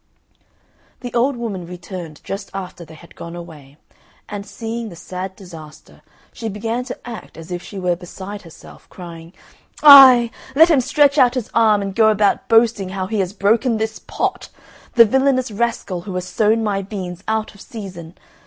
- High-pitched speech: Yes, high, 205 Hz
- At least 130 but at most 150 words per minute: No, average, 175 wpm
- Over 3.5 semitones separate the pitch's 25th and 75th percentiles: Yes, average, 4.4 semitones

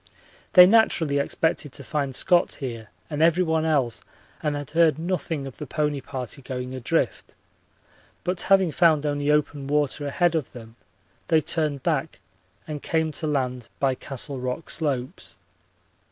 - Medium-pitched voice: Yes, medium, 150 Hz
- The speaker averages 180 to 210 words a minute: No, average, 150 wpm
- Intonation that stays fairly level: No, average, 3.2 semitones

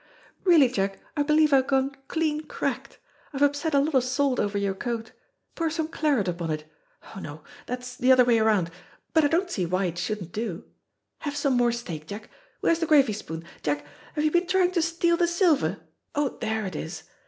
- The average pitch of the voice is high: Yes, very high, 255 Hz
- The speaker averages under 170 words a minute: No, fast, 205 wpm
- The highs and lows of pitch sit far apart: Yes, wide, 7.5 semitones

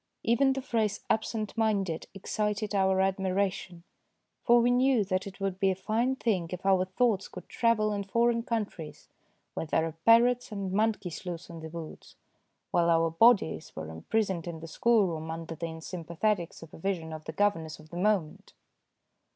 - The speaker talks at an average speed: Yes, average, 180 wpm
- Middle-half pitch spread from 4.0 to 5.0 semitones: Yes, average, 4.7 semitones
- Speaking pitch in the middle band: No, high, 195 Hz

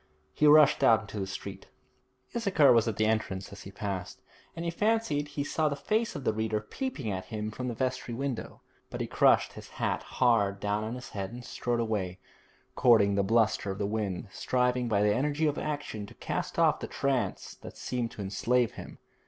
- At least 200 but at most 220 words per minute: Yes, fast, 205 wpm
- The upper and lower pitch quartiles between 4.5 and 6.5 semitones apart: Yes, average, 5.2 semitones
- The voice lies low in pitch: Yes, low, 115 Hz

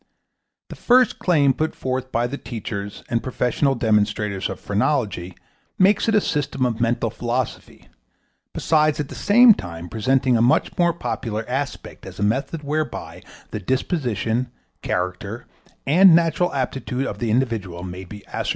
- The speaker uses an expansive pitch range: Yes, wide, 5.7 semitones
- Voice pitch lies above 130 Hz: No, low, 125 Hz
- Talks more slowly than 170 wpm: Yes, average, 150 wpm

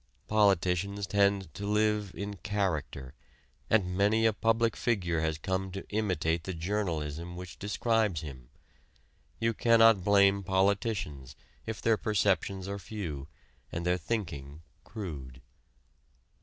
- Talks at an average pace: No, slow, 120 wpm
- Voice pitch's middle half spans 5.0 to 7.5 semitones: No, average, 4.1 semitones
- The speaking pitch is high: No, very low, 95 Hz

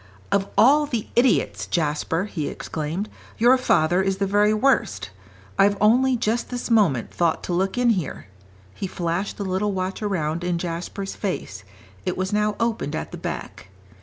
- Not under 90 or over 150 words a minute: No, average, 165 wpm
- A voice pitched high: Yes, high, 195 Hz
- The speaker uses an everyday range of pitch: Yes, average, 4.2 semitones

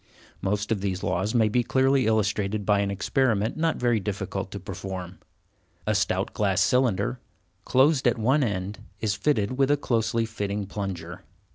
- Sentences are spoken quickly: No, average, 160 wpm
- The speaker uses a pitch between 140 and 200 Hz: No, low, 105 Hz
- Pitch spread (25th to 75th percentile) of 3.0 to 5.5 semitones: Yes, average, 3.9 semitones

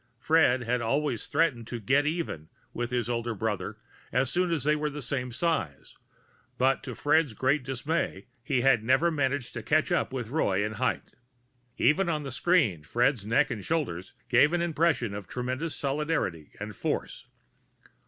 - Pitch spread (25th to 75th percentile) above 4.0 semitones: Yes, average, 4.6 semitones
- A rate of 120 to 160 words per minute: No, average, 170 wpm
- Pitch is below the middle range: Yes, low, 130 Hz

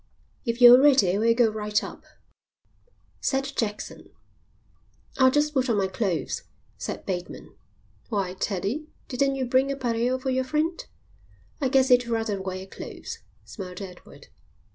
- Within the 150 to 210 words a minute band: No, average, 140 wpm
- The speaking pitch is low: No, high, 240 Hz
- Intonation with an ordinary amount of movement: Yes, average, 4.9 semitones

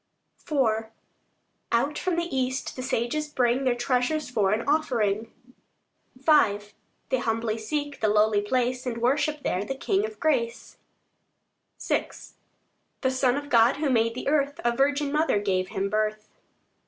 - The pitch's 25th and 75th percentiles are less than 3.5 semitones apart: No, average, 4.5 semitones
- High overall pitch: Yes, very high, 250 Hz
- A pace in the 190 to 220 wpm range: No, average, 150 wpm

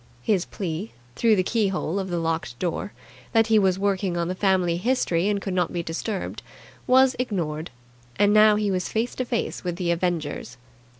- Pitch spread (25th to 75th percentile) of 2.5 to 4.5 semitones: Yes, average, 3.6 semitones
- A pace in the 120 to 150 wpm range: No, average, 185 wpm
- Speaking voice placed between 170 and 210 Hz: Yes, high, 190 Hz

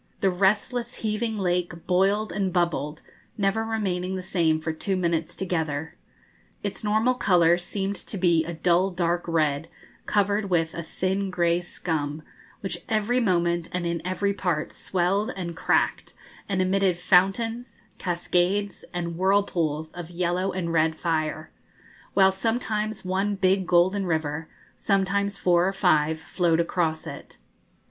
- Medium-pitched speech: Yes, medium, 180 Hz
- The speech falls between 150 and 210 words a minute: No, average, 140 wpm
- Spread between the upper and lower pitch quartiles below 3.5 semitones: Yes, average, 2.7 semitones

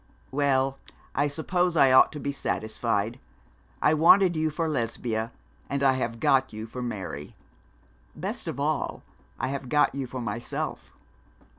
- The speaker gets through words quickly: No, average, 150 wpm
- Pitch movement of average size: Yes, average, 4.0 semitones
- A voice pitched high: No, low, 135 Hz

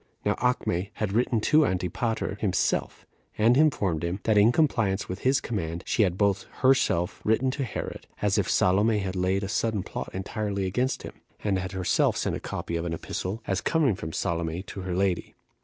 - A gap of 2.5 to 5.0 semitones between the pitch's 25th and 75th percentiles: Yes, average, 3.6 semitones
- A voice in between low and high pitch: No, low, 100 Hz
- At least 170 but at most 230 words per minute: Yes, average, 190 wpm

